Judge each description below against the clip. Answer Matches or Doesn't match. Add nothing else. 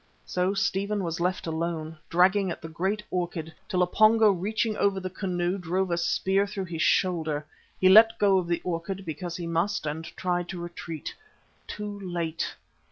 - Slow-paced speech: Doesn't match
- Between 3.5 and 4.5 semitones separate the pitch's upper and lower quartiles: Doesn't match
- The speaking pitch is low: Doesn't match